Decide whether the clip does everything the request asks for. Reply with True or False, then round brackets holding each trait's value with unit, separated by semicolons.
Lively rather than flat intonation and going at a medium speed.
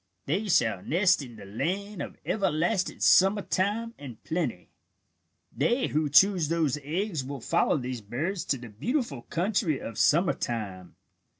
True (7.6 semitones; 145 wpm)